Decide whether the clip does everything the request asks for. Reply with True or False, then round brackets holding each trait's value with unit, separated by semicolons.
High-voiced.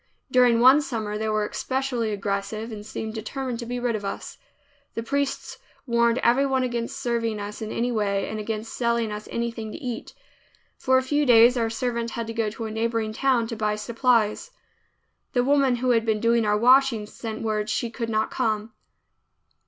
True (230 Hz)